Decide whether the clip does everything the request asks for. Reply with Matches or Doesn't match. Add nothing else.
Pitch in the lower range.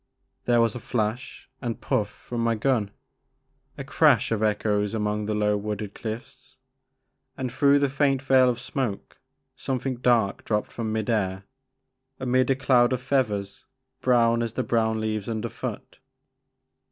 Matches